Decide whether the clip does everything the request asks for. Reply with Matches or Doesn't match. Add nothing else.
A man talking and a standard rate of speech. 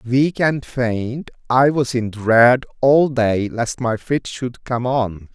Matches